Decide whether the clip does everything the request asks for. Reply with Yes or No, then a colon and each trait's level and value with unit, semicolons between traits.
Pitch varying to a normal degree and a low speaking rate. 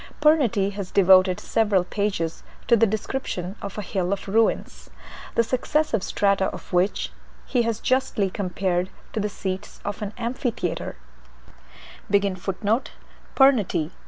Yes: average, 3.3 semitones; slow, 120 wpm